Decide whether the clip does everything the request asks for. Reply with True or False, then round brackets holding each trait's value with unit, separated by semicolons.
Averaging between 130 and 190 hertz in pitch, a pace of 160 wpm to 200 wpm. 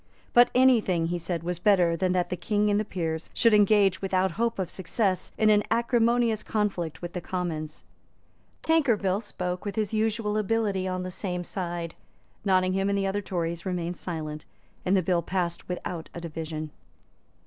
True (185 Hz; 175 wpm)